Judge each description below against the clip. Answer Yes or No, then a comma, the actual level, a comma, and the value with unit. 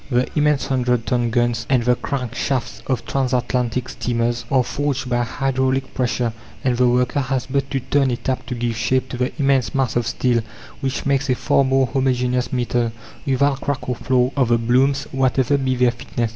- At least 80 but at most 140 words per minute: No, average, 195 wpm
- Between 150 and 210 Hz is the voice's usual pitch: No, low, 125 Hz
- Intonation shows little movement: Yes, narrow, 1.8 semitones